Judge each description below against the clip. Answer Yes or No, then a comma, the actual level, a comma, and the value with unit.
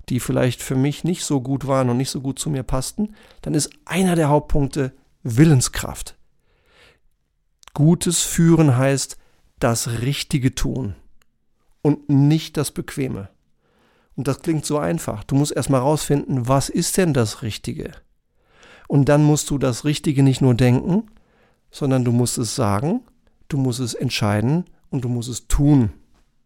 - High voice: No, medium, 140 Hz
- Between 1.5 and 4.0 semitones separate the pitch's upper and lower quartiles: Yes, average, 3.3 semitones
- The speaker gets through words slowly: No, average, 155 wpm